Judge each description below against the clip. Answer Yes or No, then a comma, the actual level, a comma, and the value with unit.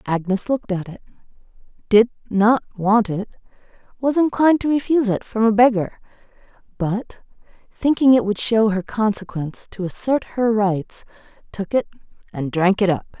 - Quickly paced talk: No, average, 150 wpm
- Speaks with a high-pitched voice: Yes, high, 215 Hz